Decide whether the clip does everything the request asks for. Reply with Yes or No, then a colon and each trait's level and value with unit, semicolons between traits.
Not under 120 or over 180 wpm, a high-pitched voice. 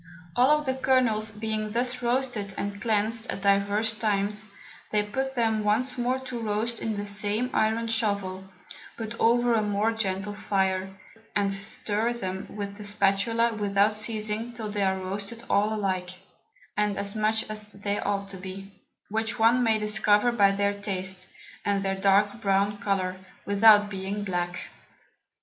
Yes: average, 155 wpm; high, 210 Hz